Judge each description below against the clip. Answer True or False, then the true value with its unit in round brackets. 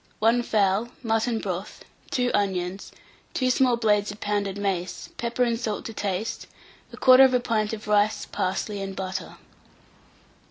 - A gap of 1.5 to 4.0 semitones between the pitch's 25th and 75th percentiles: True (3.1 semitones)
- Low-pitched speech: False (210 Hz)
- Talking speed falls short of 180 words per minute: True (135 wpm)